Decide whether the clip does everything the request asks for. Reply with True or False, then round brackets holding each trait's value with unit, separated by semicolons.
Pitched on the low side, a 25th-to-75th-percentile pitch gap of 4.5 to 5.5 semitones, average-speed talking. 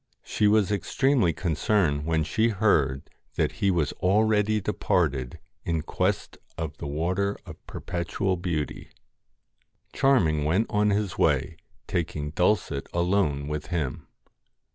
False (90 Hz; 5.2 semitones; 120 wpm)